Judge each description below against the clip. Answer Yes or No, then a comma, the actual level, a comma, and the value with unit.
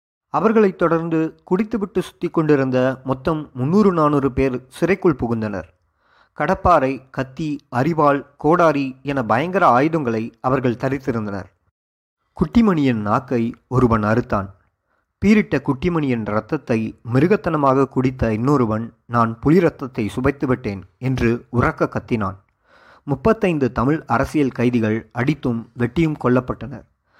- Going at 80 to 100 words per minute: Yes, average, 95 wpm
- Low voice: Yes, low, 130 Hz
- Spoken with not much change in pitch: No, average, 5.3 semitones